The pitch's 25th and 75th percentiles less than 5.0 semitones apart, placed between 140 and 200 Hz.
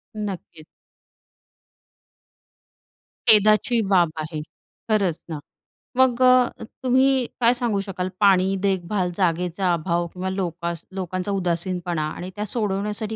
Yes: average, 3.5 semitones; high, 190 Hz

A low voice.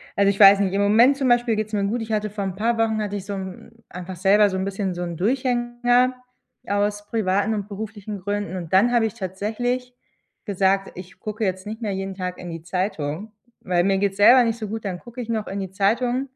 No: high, 205 Hz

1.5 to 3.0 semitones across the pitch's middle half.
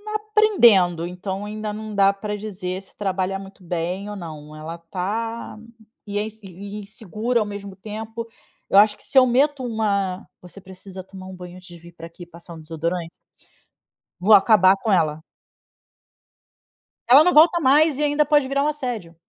No: average, 4.0 semitones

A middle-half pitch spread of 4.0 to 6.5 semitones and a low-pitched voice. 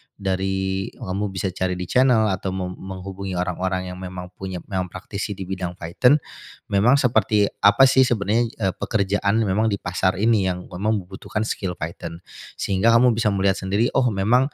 No: average, 2.9 semitones; very low, 95 Hz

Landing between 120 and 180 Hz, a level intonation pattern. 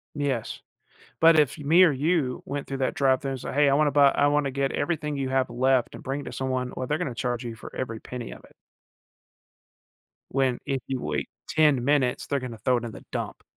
Yes: low, 135 Hz; narrow, 2.2 semitones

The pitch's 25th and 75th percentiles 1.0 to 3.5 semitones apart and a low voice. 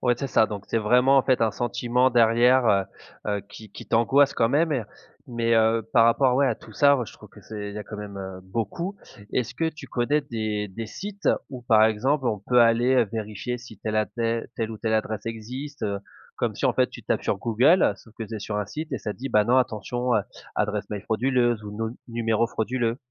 Yes: average, 2.8 semitones; low, 115 Hz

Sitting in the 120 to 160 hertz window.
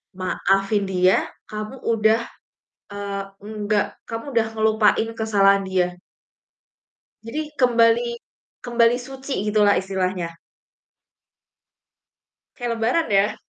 No: high, 215 Hz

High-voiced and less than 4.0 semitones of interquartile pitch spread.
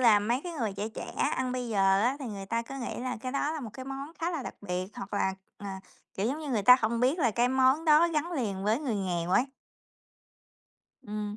No: high, 245 Hz; average, 4.8 semitones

